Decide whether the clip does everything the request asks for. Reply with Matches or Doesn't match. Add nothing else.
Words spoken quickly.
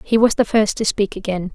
Matches